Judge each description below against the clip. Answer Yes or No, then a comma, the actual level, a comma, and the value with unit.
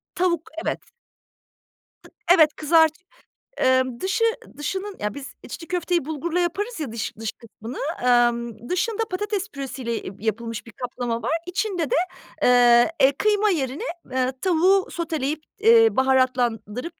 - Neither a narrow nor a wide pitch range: No, wide, 6.9 semitones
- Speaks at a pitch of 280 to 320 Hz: Yes, very high, 295 Hz